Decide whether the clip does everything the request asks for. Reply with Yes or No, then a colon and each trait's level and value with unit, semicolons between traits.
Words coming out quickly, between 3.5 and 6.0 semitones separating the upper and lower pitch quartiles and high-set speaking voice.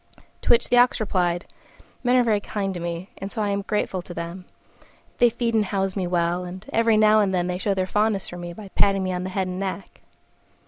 No: fast, 240 wpm; average, 3.0 semitones; high, 195 Hz